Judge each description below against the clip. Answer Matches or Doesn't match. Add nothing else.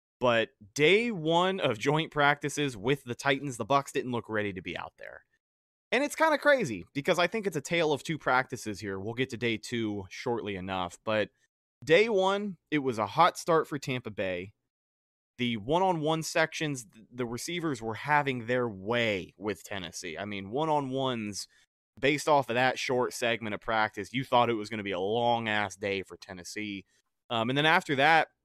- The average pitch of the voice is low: Matches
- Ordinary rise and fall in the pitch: Doesn't match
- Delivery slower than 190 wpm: Doesn't match